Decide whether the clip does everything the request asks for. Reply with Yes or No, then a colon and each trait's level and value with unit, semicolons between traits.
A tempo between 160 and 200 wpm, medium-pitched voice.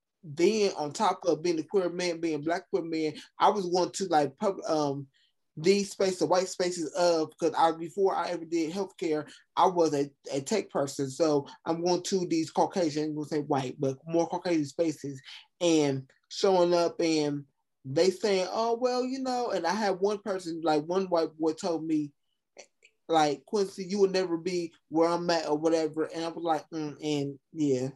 Yes: average, 195 wpm; medium, 165 Hz